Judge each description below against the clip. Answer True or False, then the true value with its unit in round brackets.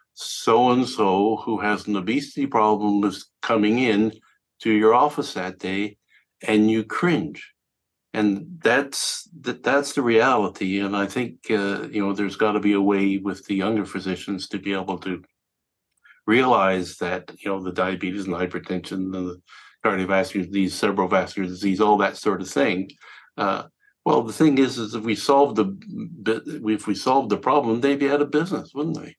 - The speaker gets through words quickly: False (175 wpm)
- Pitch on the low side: True (105 Hz)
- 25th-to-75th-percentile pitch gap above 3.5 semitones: True (4.4 semitones)